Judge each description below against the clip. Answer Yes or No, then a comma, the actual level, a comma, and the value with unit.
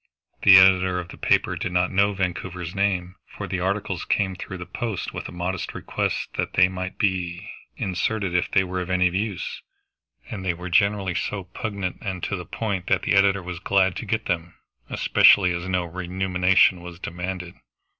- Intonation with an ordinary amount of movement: No, narrow, 1.5 semitones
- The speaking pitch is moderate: No, very low, 95 Hz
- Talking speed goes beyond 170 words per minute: Yes, average, 185 wpm